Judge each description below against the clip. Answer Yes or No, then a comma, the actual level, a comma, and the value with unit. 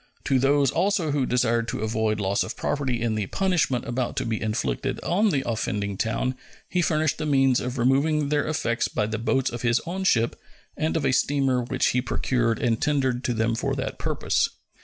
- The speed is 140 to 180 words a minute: No, average, 200 wpm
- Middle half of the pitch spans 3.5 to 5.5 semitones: Yes, average, 4.0 semitones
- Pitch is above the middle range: No, low, 125 Hz